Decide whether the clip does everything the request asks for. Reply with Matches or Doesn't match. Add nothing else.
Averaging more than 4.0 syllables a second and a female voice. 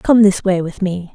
Matches